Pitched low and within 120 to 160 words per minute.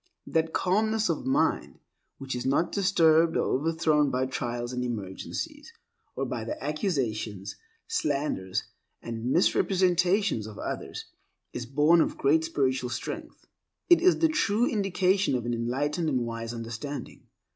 No: medium, 150 Hz; slow, 135 wpm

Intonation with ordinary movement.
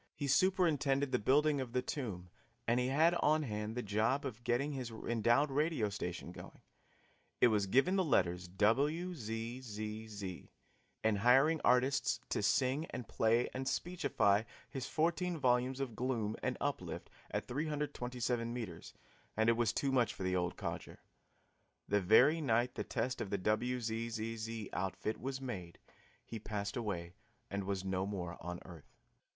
Yes: average, 4.6 semitones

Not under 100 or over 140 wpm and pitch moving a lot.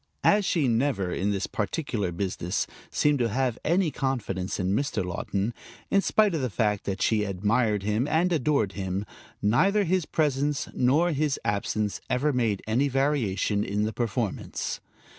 No: average, 160 wpm; wide, 6.4 semitones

